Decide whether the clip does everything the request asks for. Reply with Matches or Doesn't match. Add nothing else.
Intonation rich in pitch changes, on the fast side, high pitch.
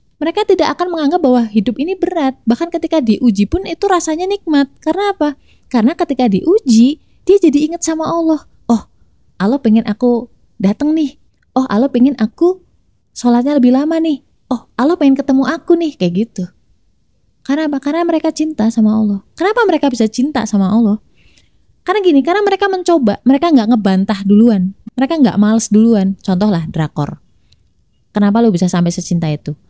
Matches